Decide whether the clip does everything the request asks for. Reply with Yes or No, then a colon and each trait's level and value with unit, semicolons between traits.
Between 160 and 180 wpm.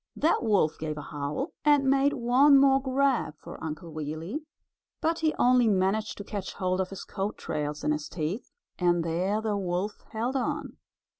Yes: average, 175 wpm